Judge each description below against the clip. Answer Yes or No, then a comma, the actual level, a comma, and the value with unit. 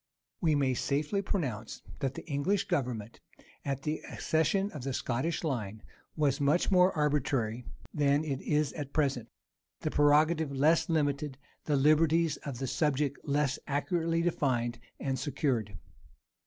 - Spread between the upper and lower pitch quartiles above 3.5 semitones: No, average, 2.9 semitones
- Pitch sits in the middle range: Yes, medium, 145 Hz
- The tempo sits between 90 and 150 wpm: Yes, average, 140 wpm